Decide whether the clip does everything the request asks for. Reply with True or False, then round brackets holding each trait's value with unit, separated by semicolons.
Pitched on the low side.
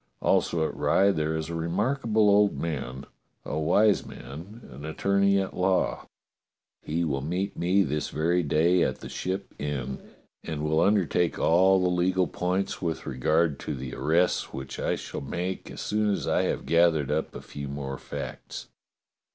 True (85 Hz)